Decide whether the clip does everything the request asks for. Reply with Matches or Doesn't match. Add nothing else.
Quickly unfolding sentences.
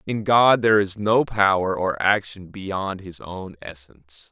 Doesn't match